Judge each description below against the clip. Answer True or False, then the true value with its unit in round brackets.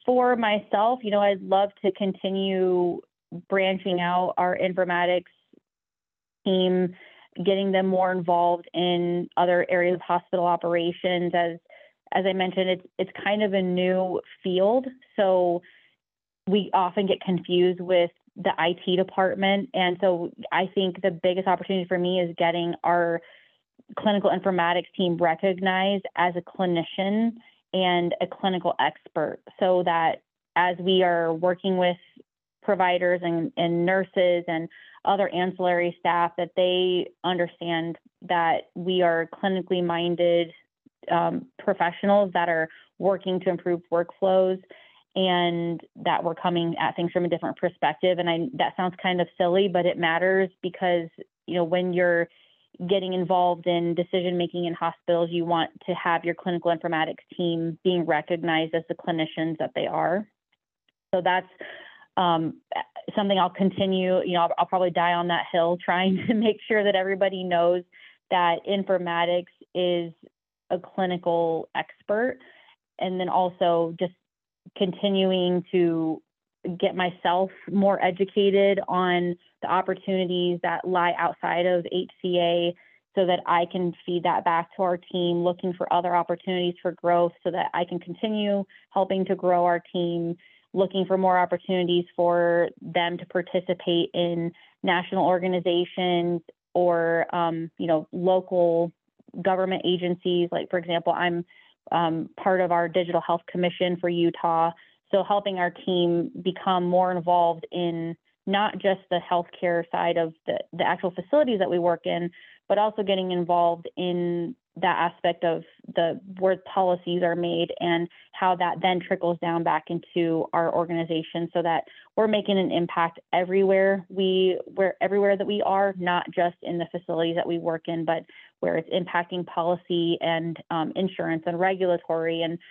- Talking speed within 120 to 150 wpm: True (145 wpm)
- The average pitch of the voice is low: False (180 Hz)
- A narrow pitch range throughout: True (1.5 semitones)